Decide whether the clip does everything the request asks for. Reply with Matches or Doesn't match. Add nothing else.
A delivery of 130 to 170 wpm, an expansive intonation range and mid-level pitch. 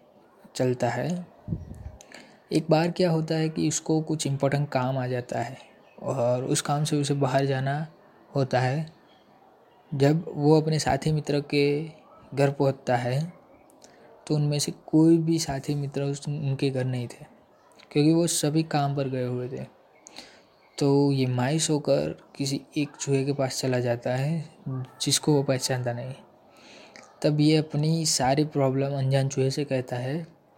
Doesn't match